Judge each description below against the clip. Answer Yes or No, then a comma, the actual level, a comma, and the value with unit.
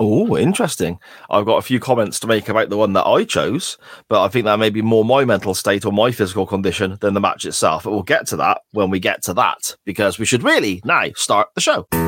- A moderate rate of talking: No, fast, 255 wpm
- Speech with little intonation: Yes, narrow, 1.7 semitones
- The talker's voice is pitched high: No, low, 110 Hz